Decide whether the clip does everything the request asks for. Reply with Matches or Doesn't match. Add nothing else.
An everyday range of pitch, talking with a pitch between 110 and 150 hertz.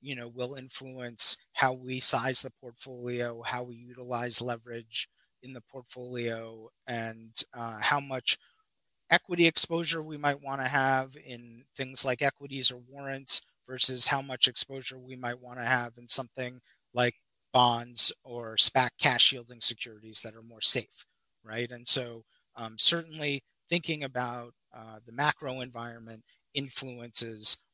Doesn't match